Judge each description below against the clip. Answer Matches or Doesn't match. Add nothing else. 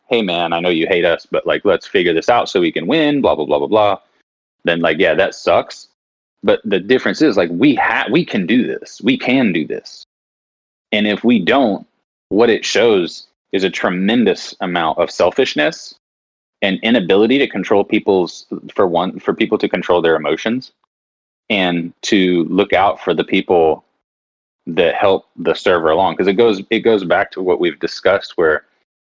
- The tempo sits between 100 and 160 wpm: Doesn't match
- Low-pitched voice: Matches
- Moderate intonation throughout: Doesn't match